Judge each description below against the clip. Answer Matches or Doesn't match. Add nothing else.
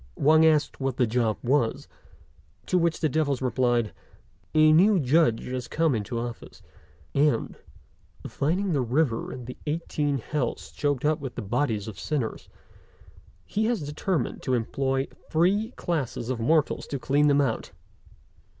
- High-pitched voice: Doesn't match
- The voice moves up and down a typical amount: Matches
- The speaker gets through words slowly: Doesn't match